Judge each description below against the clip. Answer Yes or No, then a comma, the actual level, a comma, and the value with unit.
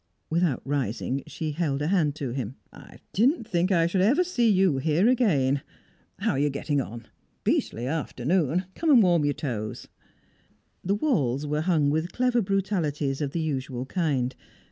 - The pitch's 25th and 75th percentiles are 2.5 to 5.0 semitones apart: No, wide, 5.6 semitones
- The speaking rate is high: No, average, 165 wpm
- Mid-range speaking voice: Yes, medium, 155 Hz